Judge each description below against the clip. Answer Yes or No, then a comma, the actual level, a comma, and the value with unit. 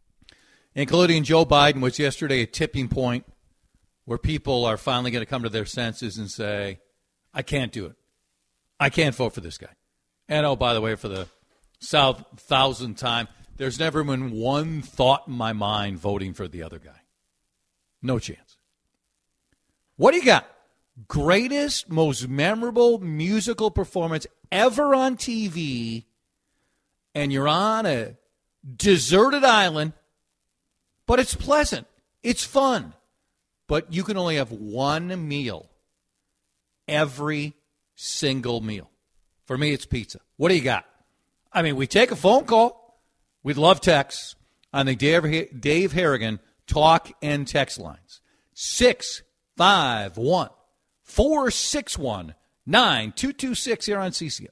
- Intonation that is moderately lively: No, wide, 7.4 semitones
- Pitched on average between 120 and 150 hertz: Yes, medium, 145 Hz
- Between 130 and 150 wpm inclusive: Yes, average, 140 wpm